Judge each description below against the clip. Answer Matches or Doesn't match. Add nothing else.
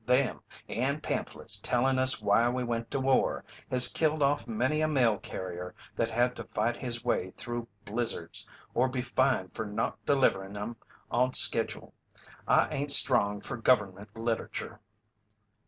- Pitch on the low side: Matches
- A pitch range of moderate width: Matches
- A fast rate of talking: Doesn't match